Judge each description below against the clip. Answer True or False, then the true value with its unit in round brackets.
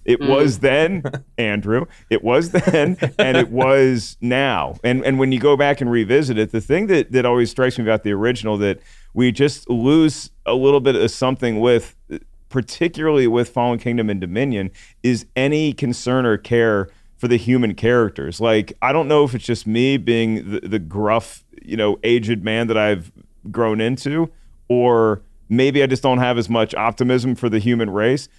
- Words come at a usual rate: True (185 wpm)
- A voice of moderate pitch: False (120 Hz)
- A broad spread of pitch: False (3.3 semitones)